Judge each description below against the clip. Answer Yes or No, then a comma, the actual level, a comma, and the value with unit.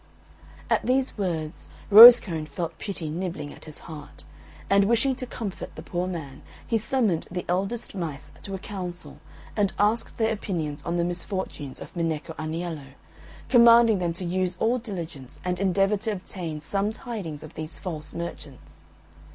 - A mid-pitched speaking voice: Yes, medium, 180 Hz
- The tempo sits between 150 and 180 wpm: Yes, average, 160 wpm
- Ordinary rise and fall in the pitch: Yes, average, 4.5 semitones